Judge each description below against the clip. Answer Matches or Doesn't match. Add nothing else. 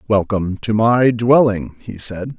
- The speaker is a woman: Doesn't match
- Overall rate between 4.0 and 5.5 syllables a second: Matches